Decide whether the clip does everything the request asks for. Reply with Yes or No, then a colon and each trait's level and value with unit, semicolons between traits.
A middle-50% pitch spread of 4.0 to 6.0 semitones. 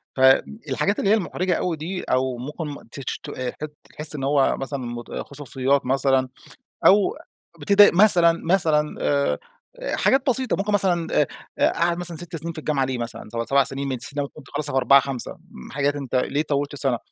Yes: average, 4.4 semitones